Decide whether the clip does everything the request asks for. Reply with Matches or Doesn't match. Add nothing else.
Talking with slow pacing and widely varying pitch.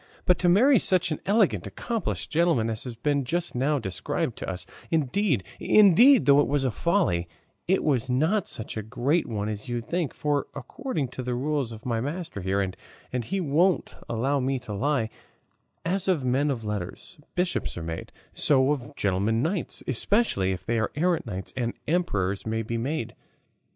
Doesn't match